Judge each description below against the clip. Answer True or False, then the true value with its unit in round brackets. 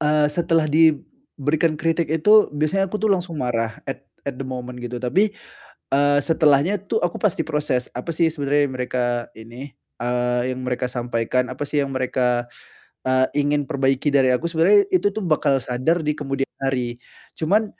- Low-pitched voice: False (145 Hz)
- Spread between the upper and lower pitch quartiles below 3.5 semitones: False (4.4 semitones)